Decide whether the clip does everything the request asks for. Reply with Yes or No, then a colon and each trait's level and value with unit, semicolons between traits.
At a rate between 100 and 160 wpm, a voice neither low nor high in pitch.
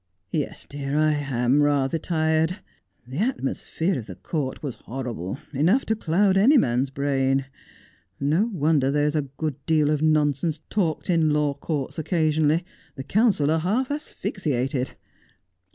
Yes: average, 150 wpm; medium, 150 Hz